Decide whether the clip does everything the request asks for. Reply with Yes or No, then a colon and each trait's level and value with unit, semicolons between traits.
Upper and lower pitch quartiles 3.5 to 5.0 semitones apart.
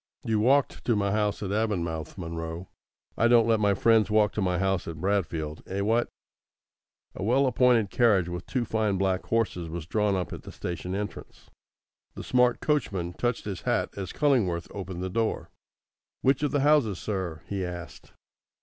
Yes: average, 4.3 semitones